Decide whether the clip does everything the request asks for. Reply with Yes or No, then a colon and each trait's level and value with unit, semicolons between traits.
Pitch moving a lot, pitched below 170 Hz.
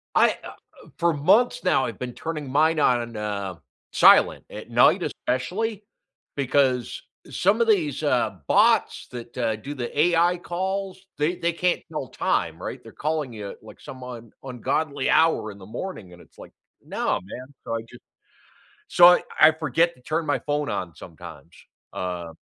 Yes: wide, 6.4 semitones; medium, 140 Hz